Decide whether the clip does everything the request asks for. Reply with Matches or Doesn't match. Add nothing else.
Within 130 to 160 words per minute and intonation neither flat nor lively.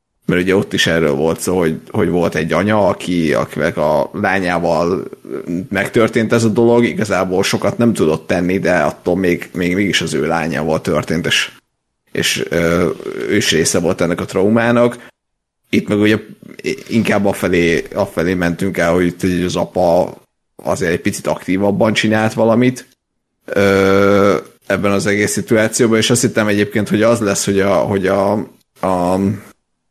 Matches